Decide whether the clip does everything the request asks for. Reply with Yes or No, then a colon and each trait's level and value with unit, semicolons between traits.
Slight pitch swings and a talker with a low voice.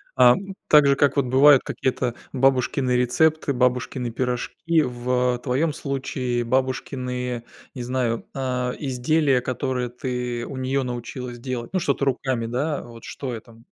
Yes: narrow, 1.8 semitones; low, 125 Hz